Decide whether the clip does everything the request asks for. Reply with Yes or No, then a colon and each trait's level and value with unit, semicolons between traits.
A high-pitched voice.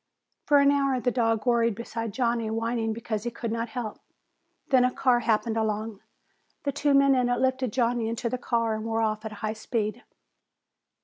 Yes: high, 230 Hz